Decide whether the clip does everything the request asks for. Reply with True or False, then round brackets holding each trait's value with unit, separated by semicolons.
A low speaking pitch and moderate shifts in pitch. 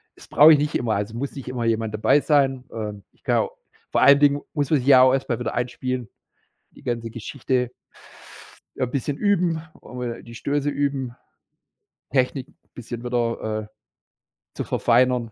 True (125 Hz; 3.1 semitones)